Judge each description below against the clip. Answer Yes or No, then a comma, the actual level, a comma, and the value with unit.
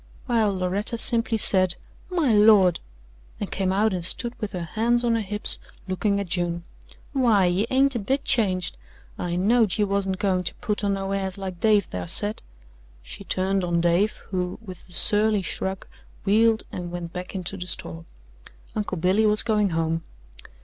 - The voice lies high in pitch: Yes, high, 195 Hz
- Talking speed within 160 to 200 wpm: Yes, average, 180 wpm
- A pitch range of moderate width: Yes, average, 3.1 semitones